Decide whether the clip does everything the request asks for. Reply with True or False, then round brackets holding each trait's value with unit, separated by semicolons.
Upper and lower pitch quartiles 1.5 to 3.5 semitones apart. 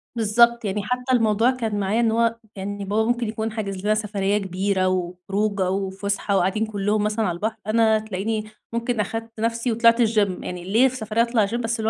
True (2.4 semitones)